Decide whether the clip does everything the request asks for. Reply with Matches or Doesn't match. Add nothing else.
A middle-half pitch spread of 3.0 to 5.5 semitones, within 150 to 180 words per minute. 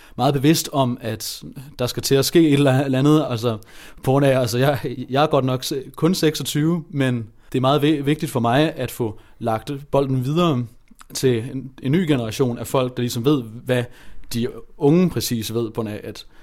Doesn't match